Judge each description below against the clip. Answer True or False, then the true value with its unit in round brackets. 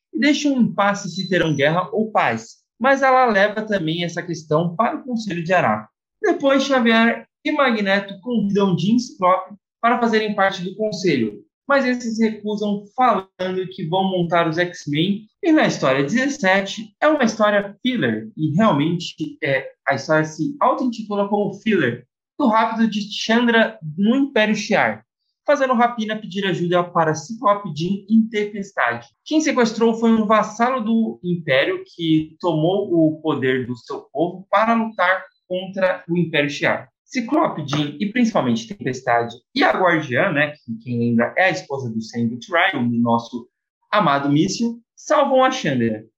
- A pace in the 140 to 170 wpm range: True (150 wpm)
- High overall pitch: True (195 Hz)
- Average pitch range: False (6.0 semitones)